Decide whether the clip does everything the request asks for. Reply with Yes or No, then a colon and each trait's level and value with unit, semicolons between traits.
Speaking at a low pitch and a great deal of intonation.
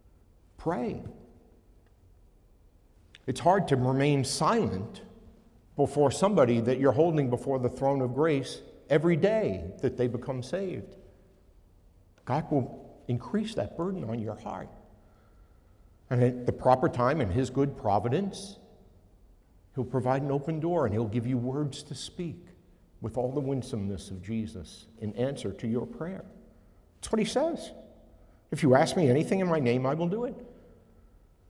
Yes: low, 125 Hz; wide, 6.3 semitones